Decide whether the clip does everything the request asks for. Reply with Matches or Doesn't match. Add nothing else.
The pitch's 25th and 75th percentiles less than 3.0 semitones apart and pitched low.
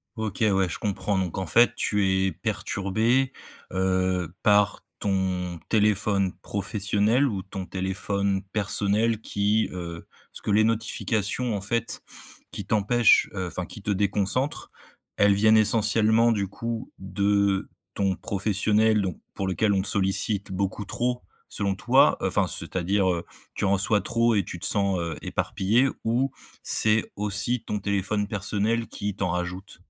Matches